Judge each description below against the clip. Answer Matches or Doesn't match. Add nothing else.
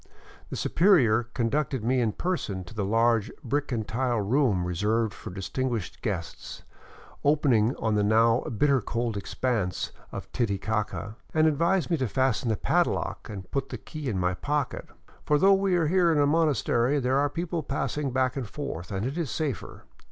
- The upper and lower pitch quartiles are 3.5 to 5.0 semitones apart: Doesn't match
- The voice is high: Doesn't match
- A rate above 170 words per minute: Matches